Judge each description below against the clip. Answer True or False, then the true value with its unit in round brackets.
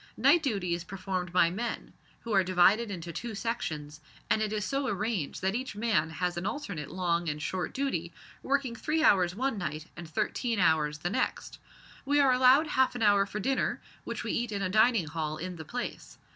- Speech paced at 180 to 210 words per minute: True (200 wpm)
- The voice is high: True (195 Hz)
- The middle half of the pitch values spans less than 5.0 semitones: False (5.6 semitones)